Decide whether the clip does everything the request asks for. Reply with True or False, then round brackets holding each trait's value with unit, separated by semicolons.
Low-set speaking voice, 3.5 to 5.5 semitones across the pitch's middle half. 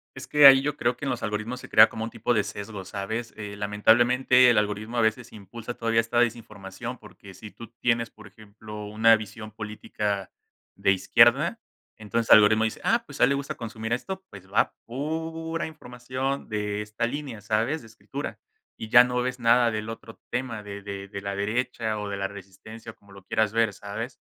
False (110 Hz; 2.9 semitones)